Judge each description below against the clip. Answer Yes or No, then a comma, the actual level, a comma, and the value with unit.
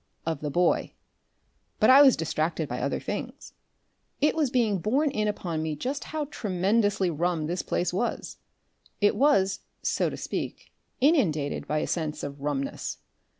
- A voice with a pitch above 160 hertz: Yes, medium, 185 Hz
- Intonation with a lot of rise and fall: Yes, wide, 7.4 semitones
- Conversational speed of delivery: Yes, average, 155 wpm